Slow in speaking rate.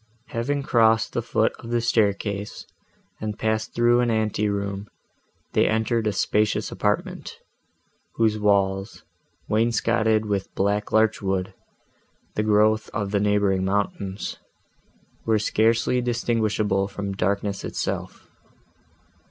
Yes: slow, 115 wpm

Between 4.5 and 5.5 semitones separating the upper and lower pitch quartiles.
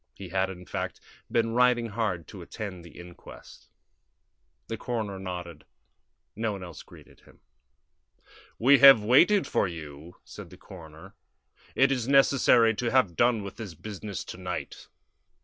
Yes: average, 5.0 semitones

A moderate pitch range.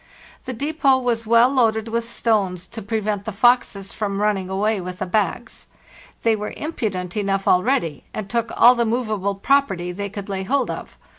Yes: average, 3.3 semitones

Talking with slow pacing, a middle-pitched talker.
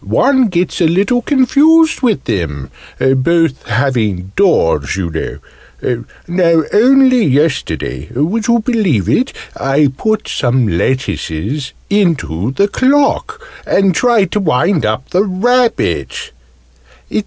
Yes: slow, 115 wpm; medium, 170 Hz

